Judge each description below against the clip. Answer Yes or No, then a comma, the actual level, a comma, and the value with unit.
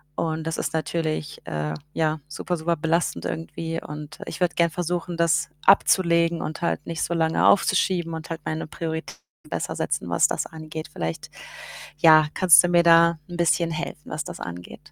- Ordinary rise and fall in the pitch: No, narrow, 1.5 semitones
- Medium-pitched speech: Yes, medium, 165 Hz